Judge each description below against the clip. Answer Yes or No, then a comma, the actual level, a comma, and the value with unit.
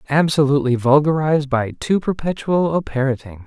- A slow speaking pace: Yes, slow, 120 wpm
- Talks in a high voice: No, medium, 145 Hz